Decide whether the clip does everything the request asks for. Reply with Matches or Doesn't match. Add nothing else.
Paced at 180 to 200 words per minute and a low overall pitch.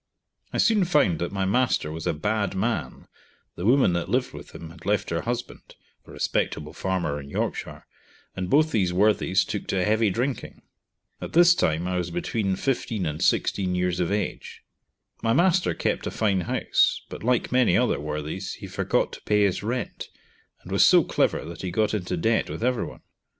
Matches